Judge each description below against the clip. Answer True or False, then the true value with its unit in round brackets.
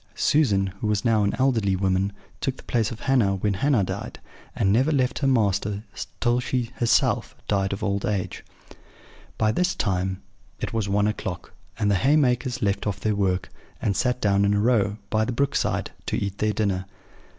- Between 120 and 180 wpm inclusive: False (190 wpm)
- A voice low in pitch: True (105 Hz)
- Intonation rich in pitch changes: False (3.8 semitones)